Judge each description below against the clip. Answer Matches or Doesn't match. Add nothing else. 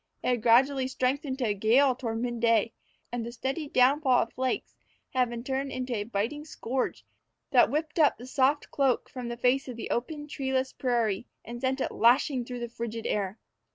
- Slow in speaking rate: Doesn't match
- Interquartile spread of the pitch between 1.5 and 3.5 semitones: Matches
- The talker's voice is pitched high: Matches